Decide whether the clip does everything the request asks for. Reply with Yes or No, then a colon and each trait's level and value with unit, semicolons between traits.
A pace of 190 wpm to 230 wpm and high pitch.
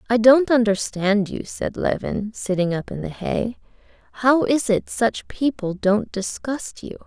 No: average, 160 wpm; high, 225 Hz